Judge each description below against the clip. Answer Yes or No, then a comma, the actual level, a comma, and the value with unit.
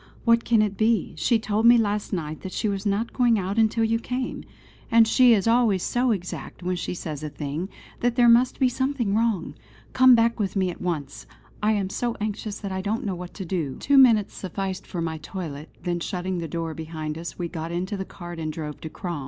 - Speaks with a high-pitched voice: Yes, high, 195 Hz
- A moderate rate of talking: No, fast, 225 wpm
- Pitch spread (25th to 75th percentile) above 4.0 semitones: Yes, average, 5.0 semitones